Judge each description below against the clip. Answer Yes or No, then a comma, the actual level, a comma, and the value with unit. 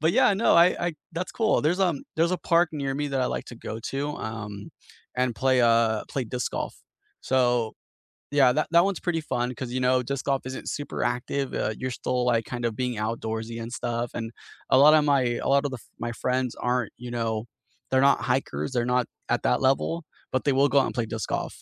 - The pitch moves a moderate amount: Yes, average, 3.3 semitones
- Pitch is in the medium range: No, low, 130 Hz